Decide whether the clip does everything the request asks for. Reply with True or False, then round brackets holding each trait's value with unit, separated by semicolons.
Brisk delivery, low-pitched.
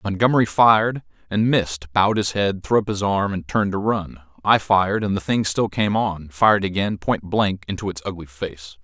True (210 wpm; 100 Hz)